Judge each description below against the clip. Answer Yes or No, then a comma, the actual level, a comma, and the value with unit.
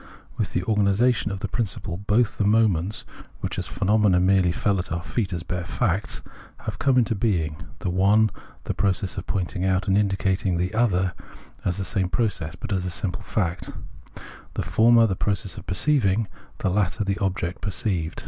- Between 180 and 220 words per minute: Yes, average, 185 wpm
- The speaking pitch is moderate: No, very low, 95 Hz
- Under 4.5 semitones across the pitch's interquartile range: Yes, average, 2.8 semitones